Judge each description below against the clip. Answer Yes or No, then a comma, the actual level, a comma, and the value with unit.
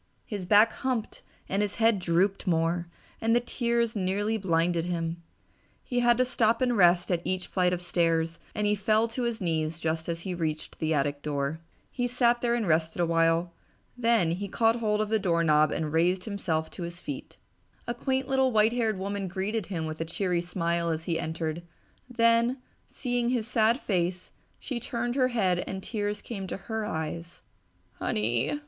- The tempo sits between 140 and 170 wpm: No, average, 180 wpm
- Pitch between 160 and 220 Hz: Yes, high, 190 Hz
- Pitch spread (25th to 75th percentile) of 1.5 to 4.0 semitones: No, wide, 5.5 semitones